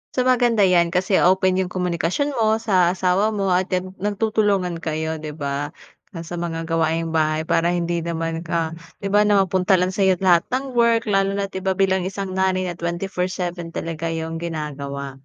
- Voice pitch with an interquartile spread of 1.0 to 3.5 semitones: Yes, average, 2.9 semitones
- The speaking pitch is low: No, medium, 180 Hz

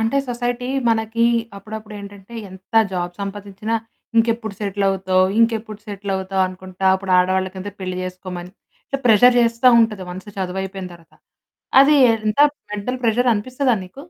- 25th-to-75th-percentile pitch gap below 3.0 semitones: No, average, 3.3 semitones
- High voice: Yes, high, 205 Hz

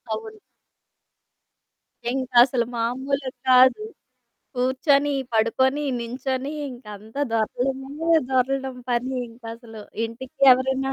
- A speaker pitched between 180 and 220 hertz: No, very high, 260 Hz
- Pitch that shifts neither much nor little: No, narrow, 2.1 semitones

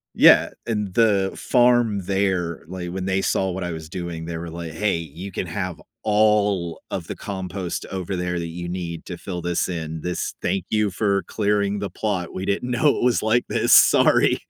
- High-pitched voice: No, very low, 95 Hz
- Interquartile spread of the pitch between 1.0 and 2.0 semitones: No, average, 2.9 semitones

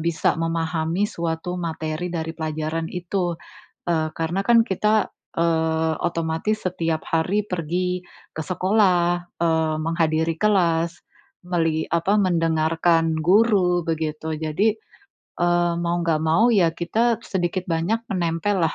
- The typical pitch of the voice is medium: Yes, medium, 170 Hz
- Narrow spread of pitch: Yes, narrow, 2.1 semitones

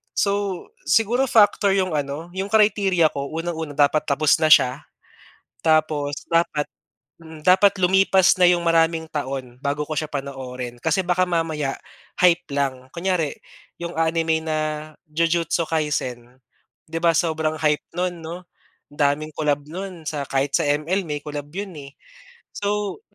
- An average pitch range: Yes, average, 3.6 semitones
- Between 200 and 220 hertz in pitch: No, medium, 160 Hz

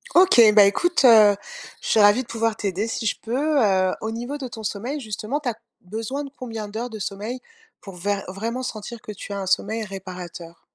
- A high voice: Yes, high, 220 Hz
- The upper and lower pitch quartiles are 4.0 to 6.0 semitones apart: No, average, 3.4 semitones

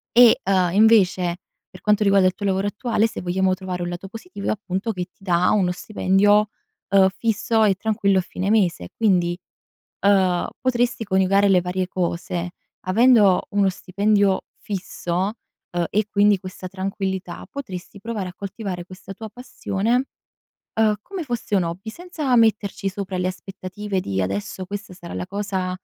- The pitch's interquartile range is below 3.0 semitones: Yes, narrow, 2.5 semitones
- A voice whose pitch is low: No, high, 195 Hz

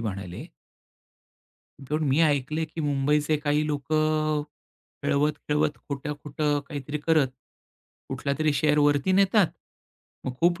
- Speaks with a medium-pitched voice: Yes, medium, 150 Hz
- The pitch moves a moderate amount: No, narrow, 1.4 semitones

